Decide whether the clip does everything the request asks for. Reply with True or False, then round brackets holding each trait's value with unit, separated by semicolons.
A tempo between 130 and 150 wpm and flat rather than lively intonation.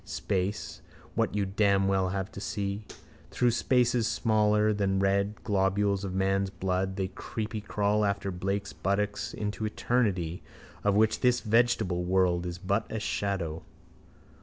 True (135 wpm; 1.8 semitones)